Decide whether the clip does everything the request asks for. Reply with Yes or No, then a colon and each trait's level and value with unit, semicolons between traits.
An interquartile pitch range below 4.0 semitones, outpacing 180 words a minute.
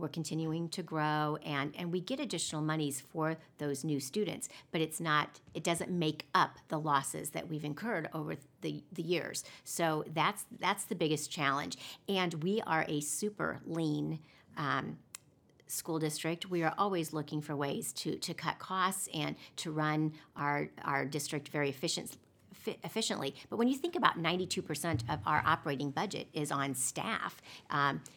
No: narrow, 2.6 semitones; average, 175 wpm